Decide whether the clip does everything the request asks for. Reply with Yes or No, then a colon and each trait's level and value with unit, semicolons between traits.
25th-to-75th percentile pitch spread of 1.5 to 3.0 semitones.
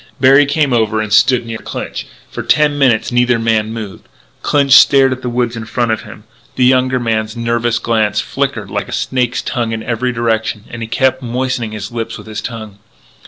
Yes: narrow, 2.4 semitones